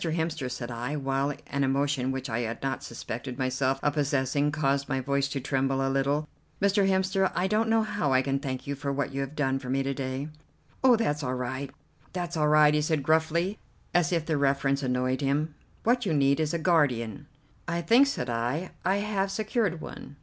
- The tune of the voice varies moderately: Yes, average, 3.8 semitones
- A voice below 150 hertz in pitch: Yes, medium, 140 Hz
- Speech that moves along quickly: Yes, fast, 210 wpm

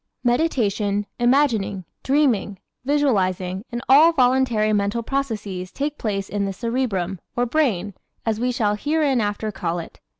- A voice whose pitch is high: Yes, high, 225 Hz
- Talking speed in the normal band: No, slow, 130 wpm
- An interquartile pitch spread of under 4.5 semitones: No, average, 4.8 semitones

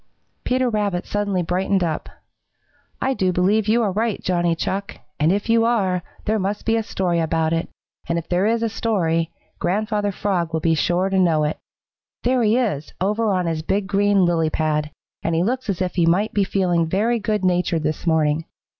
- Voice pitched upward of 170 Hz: Yes, medium, 185 Hz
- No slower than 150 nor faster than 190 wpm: No, average, 200 wpm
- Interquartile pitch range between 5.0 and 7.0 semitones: No, average, 4.0 semitones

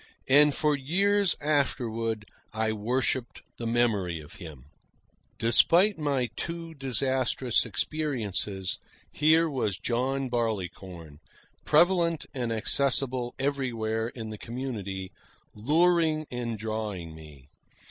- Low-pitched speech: Yes, low, 120 Hz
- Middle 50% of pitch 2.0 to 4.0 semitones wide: No, average, 5.2 semitones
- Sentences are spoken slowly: Yes, slow, 100 wpm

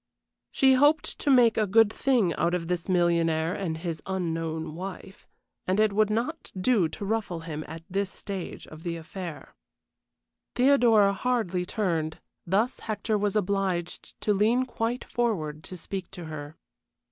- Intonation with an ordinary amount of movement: Yes, average, 4.7 semitones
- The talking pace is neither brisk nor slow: Yes, average, 155 wpm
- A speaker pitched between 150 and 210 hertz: Yes, high, 190 Hz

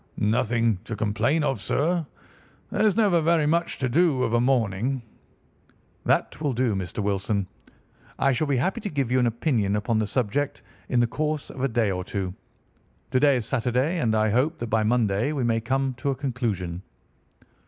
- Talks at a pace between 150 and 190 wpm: Yes, average, 185 wpm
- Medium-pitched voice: No, low, 125 Hz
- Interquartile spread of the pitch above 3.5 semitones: Yes, average, 4.6 semitones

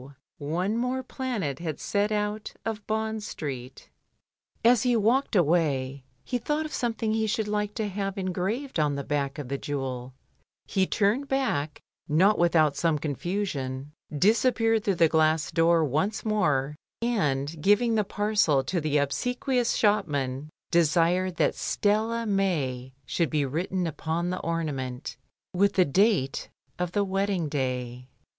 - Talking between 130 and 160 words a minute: Yes, average, 145 wpm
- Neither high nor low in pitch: Yes, medium, 180 Hz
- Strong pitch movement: Yes, wide, 6.5 semitones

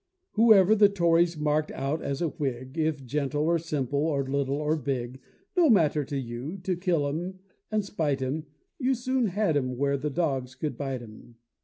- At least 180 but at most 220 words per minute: Yes, average, 190 wpm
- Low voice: No, medium, 150 Hz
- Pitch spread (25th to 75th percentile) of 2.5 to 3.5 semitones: No, average, 4.3 semitones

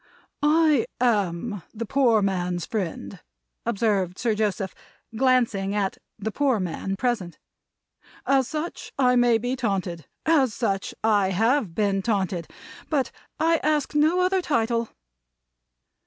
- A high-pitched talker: Yes, high, 225 Hz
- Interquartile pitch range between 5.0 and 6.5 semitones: Yes, average, 5.3 semitones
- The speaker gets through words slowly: Yes, slow, 125 wpm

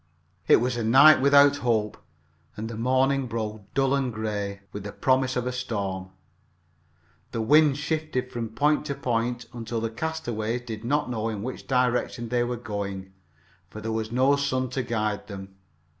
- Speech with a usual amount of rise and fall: Yes, average, 3.2 semitones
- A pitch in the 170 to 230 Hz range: No, low, 120 Hz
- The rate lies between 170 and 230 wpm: Yes, average, 175 wpm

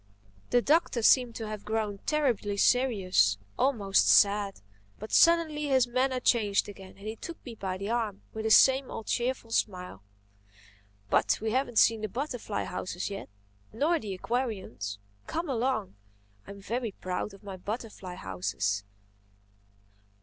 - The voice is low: No, high, 215 Hz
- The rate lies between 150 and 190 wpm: No, average, 140 wpm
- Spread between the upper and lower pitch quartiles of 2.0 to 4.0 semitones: No, average, 4.4 semitones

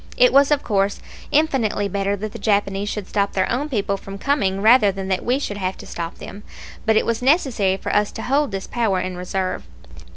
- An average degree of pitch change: Yes, average, 4.1 semitones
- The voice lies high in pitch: Yes, high, 205 Hz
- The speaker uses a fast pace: Yes, fast, 220 wpm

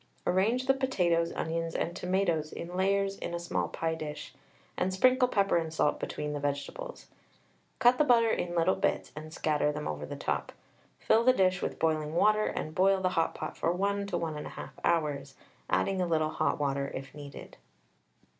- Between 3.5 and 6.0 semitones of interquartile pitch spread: Yes, average, 4.2 semitones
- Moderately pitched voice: Yes, medium, 170 Hz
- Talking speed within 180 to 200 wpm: Yes, average, 185 wpm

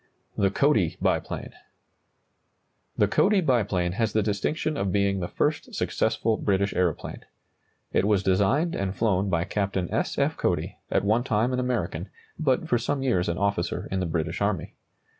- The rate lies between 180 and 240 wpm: No, average, 160 wpm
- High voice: No, low, 100 Hz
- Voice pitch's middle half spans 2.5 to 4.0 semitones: No, average, 4.5 semitones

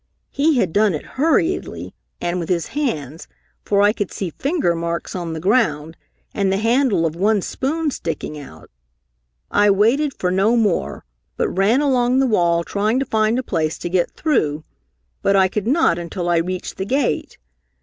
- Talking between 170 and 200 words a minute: Yes, average, 180 wpm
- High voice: Yes, high, 200 Hz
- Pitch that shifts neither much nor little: No, wide, 6.6 semitones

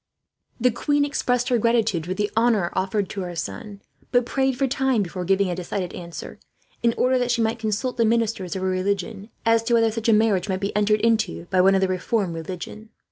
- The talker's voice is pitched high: Yes, high, 210 Hz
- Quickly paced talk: Yes, fast, 220 wpm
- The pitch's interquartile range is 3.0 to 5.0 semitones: Yes, average, 3.8 semitones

